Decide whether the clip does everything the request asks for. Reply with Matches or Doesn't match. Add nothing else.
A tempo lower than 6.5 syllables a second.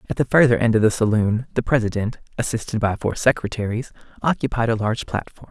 Matches